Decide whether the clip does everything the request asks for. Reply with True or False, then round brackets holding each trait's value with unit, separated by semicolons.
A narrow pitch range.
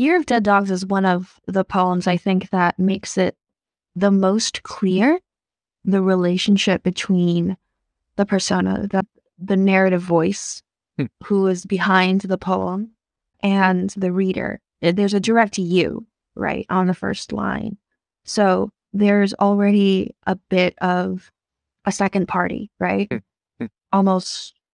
True (1.5 semitones)